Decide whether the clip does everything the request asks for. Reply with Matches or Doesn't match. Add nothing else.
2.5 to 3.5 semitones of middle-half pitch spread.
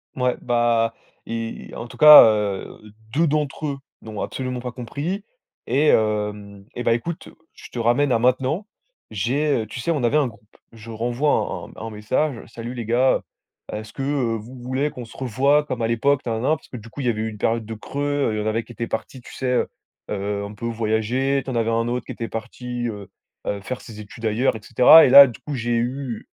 Matches